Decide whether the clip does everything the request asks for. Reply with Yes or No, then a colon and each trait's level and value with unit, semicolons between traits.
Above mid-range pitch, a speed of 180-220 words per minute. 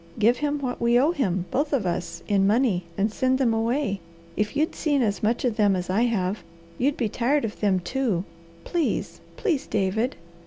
Yes: high, 230 Hz; average, 195 wpm